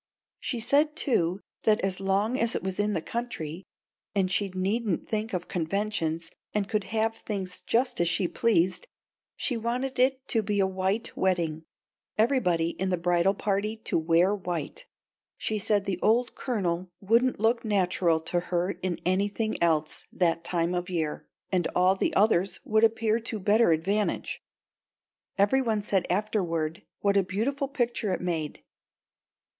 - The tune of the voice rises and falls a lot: No, average, 4.0 semitones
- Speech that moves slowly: No, average, 160 wpm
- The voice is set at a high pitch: Yes, high, 195 Hz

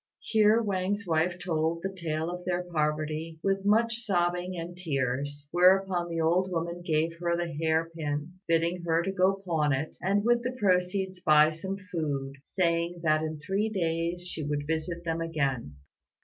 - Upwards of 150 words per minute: Yes, average, 165 wpm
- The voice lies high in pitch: No, medium, 170 Hz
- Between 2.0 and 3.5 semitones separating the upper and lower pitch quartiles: Yes, average, 2.8 semitones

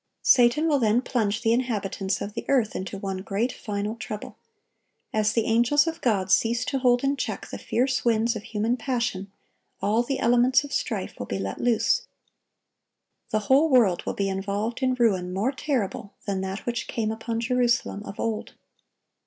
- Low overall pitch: No, high, 225 Hz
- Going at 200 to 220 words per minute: No, average, 180 wpm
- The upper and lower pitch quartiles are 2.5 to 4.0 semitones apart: Yes, average, 3.4 semitones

